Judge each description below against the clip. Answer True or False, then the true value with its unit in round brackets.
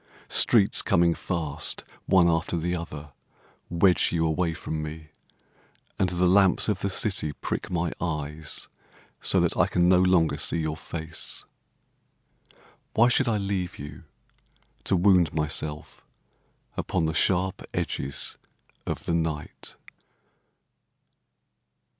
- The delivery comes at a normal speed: False (125 wpm)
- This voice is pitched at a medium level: False (85 Hz)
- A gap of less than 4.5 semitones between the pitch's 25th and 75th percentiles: True (2.7 semitones)